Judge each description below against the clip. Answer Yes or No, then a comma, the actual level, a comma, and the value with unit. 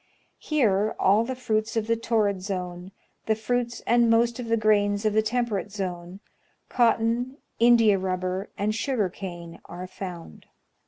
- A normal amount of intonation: Yes, average, 3.5 semitones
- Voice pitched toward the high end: Yes, high, 215 Hz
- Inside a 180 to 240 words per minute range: No, average, 150 wpm